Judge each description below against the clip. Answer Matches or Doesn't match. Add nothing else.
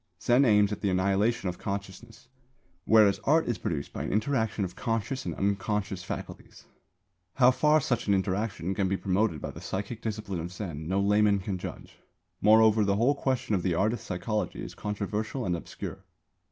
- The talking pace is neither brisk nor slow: Matches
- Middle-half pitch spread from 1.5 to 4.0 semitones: Matches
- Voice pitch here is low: Matches